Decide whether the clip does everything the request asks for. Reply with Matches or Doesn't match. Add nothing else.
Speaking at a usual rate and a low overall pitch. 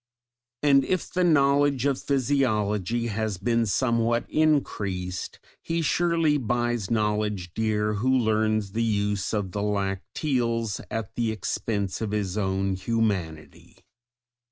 Doesn't match